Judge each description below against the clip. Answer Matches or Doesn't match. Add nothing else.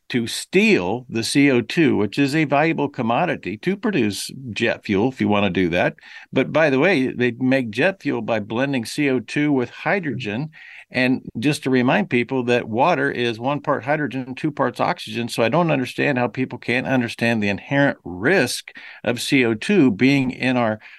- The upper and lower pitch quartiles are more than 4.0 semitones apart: Doesn't match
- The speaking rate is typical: Matches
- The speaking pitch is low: Matches